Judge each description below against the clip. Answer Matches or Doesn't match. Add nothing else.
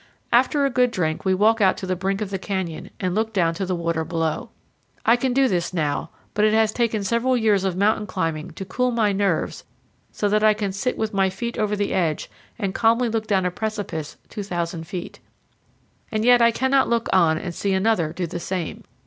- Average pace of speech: Doesn't match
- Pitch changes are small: Doesn't match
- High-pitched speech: Matches